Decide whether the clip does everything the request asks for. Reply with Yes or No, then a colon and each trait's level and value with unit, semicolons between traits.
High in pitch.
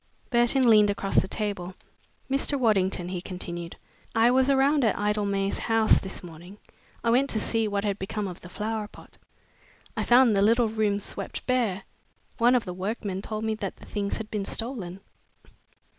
Yes: high, 210 Hz